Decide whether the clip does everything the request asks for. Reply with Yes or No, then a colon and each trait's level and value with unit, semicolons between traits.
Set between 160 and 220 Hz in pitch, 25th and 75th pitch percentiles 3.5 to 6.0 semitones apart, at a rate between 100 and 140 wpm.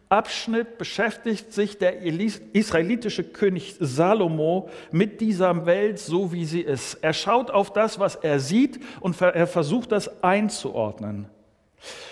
Yes: medium, 185 Hz; average, 4.2 semitones; average, 130 wpm